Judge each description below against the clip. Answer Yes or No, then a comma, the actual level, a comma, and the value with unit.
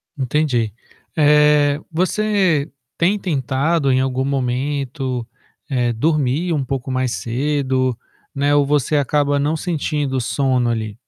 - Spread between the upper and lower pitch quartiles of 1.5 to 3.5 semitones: Yes, average, 2.7 semitones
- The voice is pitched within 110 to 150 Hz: Yes, medium, 140 Hz